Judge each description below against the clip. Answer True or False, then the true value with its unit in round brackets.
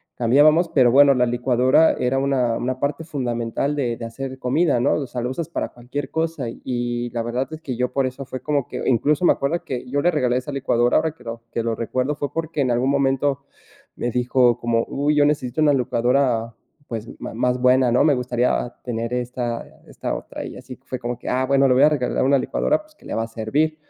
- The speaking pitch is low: True (130 Hz)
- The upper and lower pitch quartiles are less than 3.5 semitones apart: True (2.8 semitones)